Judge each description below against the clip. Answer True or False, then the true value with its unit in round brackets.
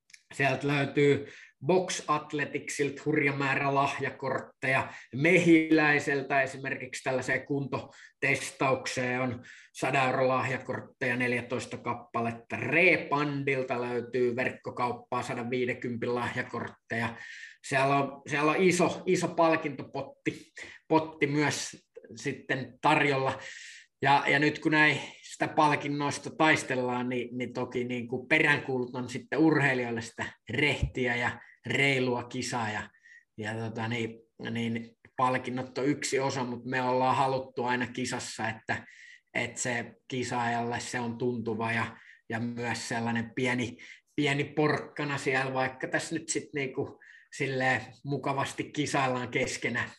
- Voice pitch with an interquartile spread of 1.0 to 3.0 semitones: True (2.7 semitones)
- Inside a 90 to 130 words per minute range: True (110 wpm)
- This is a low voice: True (130 Hz)